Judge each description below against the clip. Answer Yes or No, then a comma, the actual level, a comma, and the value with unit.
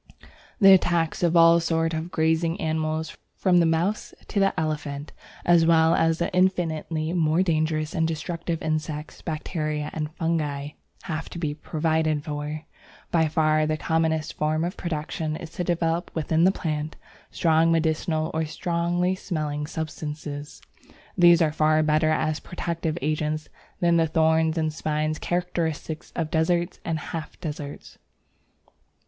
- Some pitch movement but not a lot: No, narrow, 1.5 semitones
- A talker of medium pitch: Yes, medium, 160 Hz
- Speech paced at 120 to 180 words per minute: Yes, average, 140 wpm